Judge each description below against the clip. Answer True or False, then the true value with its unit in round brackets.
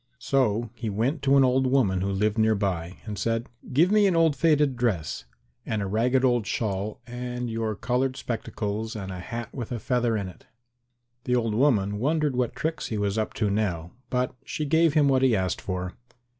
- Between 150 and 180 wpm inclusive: False (200 wpm)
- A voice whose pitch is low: True (115 Hz)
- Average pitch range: True (4.3 semitones)